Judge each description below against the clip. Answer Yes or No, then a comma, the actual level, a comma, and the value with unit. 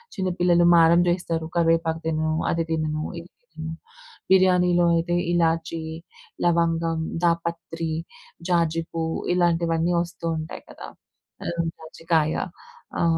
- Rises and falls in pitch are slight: Yes, narrow, 1.0 semitones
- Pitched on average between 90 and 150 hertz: No, medium, 165 Hz